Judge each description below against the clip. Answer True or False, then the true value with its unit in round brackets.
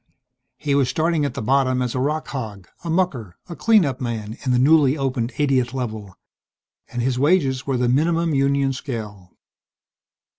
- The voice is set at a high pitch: False (130 Hz)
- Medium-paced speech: True (175 wpm)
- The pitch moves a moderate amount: True (3.4 semitones)